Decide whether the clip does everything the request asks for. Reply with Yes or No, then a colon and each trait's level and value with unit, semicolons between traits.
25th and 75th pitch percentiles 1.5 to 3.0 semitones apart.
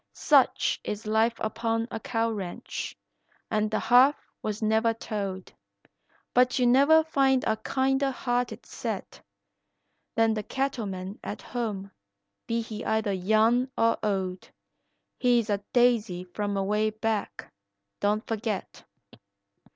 Yes: average, 2.7 semitones